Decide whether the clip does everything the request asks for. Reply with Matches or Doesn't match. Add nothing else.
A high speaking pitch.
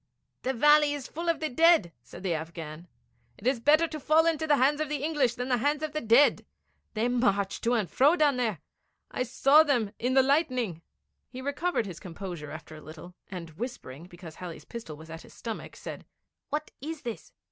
Matches